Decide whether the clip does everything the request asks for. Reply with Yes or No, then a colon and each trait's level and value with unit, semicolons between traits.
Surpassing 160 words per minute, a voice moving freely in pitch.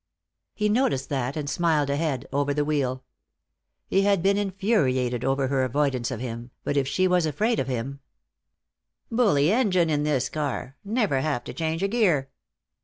Yes: average, 170 wpm; wide, 6.2 semitones